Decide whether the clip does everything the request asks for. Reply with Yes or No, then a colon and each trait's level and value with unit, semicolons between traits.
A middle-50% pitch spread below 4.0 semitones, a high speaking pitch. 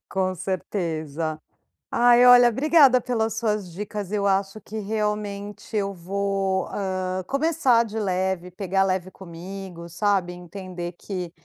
Yes: average, 2.8 semitones; high, 195 Hz